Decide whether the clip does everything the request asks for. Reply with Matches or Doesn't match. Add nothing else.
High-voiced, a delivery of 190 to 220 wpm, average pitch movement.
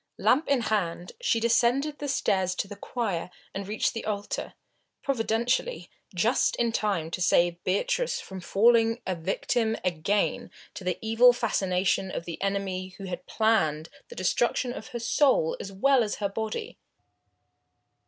Doesn't match